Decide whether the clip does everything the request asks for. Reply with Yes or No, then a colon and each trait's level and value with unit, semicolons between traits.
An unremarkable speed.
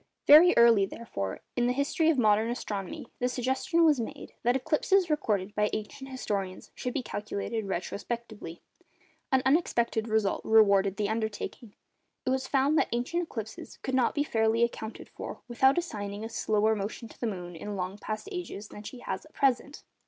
Yes: average, 175 wpm